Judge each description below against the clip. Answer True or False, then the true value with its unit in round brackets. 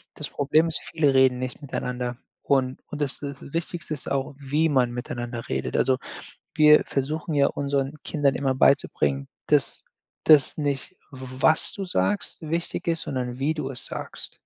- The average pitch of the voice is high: False (140 Hz)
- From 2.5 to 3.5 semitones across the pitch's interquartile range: True (2.9 semitones)